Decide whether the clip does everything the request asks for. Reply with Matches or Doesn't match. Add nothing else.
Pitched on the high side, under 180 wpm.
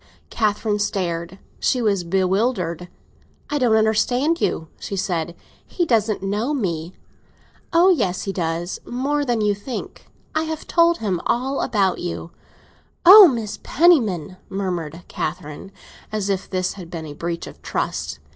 Matches